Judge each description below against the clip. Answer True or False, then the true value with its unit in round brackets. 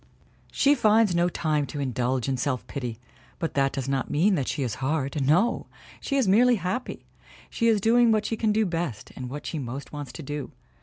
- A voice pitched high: False (155 Hz)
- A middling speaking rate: False (210 wpm)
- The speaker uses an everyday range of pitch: False (7.9 semitones)